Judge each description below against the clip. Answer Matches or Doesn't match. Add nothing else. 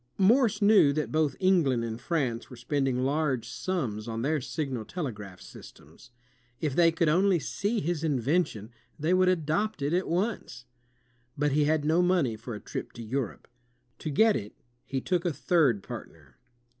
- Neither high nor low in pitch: Matches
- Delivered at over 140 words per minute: Matches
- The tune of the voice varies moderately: Doesn't match